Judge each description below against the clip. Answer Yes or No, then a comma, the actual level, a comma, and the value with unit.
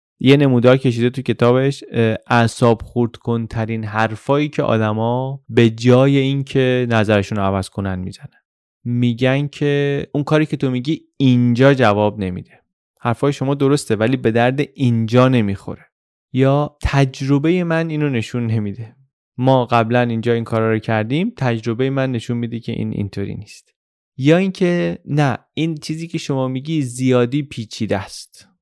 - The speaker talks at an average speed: Yes, average, 145 wpm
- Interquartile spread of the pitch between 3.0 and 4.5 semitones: Yes, average, 3.6 semitones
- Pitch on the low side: Yes, low, 125 Hz